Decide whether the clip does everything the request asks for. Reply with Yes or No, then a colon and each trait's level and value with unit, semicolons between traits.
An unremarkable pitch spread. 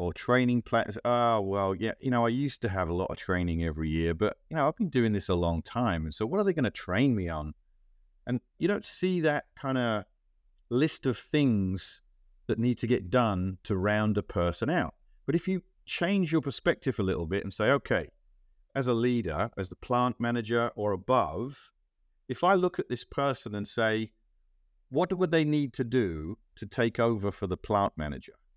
No: wide, 5.7 semitones